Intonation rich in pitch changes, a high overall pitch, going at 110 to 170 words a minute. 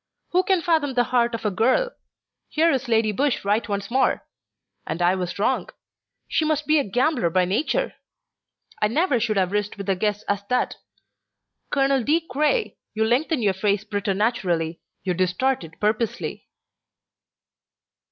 Yes: wide, 5.8 semitones; high, 225 Hz; average, 160 wpm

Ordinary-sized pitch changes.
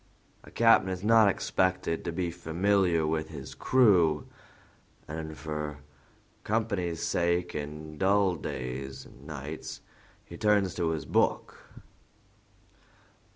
Yes: average, 3.9 semitones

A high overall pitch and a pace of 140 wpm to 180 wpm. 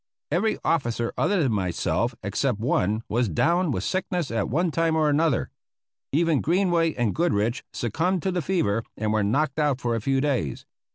No: medium, 140 Hz; average, 175 wpm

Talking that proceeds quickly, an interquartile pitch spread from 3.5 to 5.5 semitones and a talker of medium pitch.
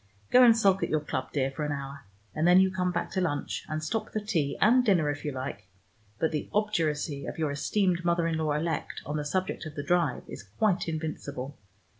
Yes: fast, 225 wpm; average, 4.3 semitones; medium, 160 Hz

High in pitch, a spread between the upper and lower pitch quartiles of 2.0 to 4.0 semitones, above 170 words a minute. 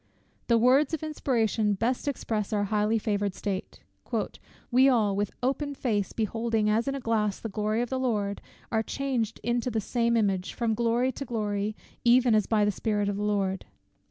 Yes: high, 225 Hz; average, 2.8 semitones; average, 185 wpm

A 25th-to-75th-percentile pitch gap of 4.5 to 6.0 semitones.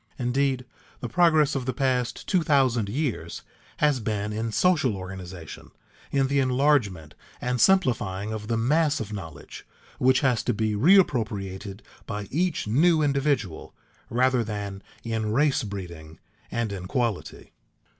Yes: average, 5.2 semitones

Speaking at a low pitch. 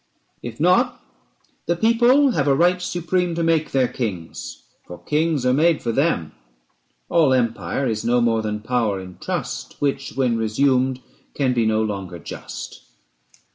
Yes: low, 130 Hz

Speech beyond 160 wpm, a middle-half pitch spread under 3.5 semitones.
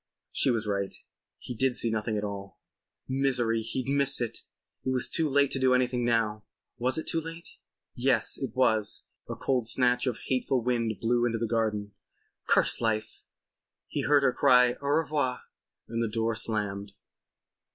Yes: average, 170 wpm; average, 2.8 semitones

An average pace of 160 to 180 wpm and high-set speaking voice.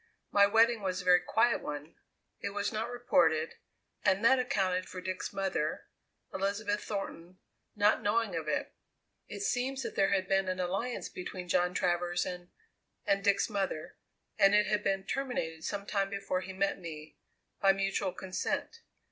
Yes: average, 165 wpm; high, 195 Hz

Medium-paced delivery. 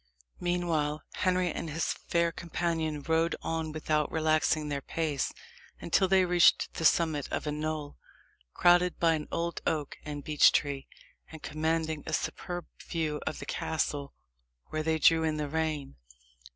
Yes: average, 150 wpm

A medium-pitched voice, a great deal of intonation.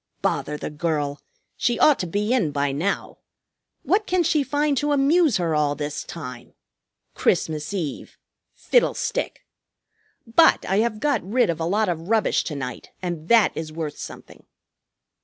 Yes: medium, 180 Hz; wide, 8.9 semitones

